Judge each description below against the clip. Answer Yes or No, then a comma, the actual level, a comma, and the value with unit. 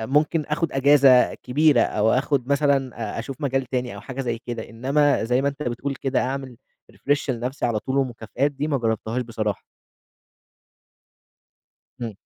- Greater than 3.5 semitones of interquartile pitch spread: No, average, 3.0 semitones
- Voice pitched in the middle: No, low, 130 Hz